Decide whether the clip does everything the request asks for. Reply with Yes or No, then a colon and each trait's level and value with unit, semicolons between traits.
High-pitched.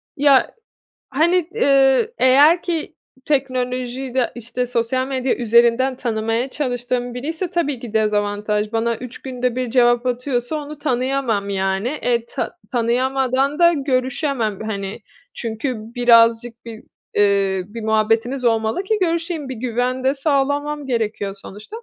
Yes: very high, 250 Hz